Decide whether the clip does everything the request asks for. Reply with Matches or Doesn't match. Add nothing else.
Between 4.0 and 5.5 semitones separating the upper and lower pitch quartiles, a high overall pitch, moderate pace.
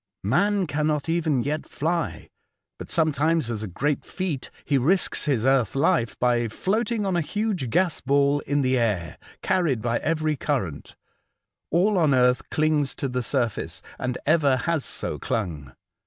Doesn't match